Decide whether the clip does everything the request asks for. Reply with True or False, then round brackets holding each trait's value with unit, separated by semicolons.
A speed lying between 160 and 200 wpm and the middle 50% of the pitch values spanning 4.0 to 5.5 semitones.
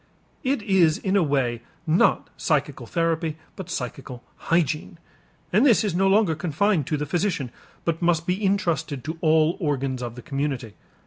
True (165 wpm; 4.6 semitones)